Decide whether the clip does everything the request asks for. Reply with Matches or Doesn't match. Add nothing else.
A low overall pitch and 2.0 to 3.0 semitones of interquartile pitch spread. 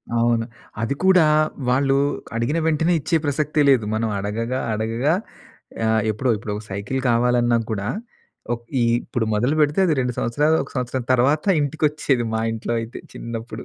Doesn't match